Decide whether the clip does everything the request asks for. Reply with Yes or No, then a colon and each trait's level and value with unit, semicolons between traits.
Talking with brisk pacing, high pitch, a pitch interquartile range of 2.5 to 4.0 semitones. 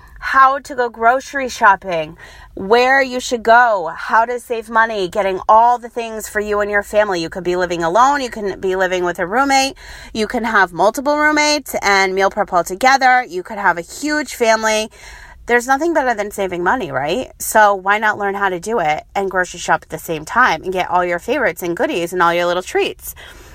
No: fast, 215 wpm; high, 210 Hz; average, 5.2 semitones